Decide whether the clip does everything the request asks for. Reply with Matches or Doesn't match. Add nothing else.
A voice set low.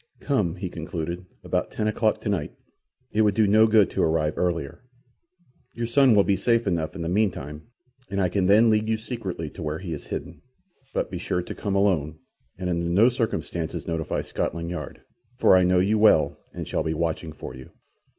Matches